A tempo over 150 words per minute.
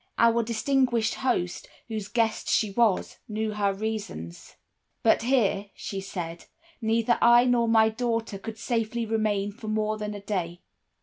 No: average, 145 wpm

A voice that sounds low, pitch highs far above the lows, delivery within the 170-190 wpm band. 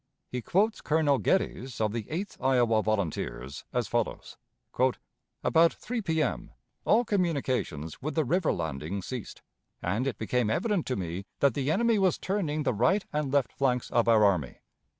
No: low, 130 Hz; wide, 7.3 semitones; average, 160 wpm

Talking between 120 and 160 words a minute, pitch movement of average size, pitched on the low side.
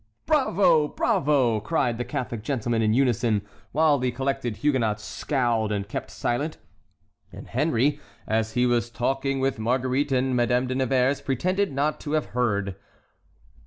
Yes: average, 150 wpm; average, 3.2 semitones; low, 125 Hz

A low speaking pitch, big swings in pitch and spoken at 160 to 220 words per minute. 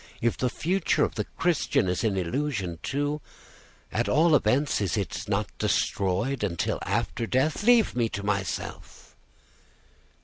No: low, 115 Hz; wide, 7.0 semitones; average, 140 wpm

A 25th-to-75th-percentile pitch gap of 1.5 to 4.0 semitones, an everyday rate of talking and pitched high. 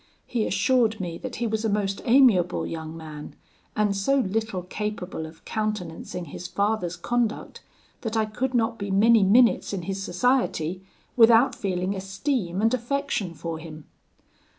No: average, 4.5 semitones; average, 150 wpm; high, 210 Hz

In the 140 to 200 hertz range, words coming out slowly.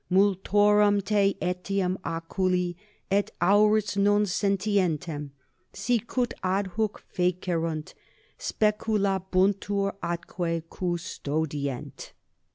Yes: high, 190 Hz; slow, 65 wpm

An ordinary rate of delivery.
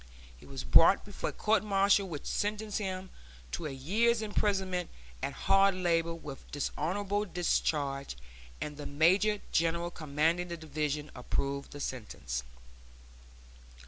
No: slow, 130 wpm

